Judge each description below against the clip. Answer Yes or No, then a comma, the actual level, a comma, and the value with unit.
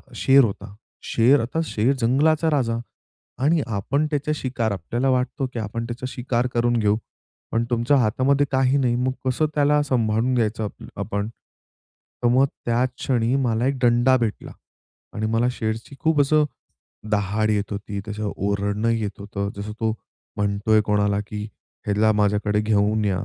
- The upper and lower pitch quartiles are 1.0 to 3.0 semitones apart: No, average, 3.7 semitones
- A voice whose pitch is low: Yes, low, 115 Hz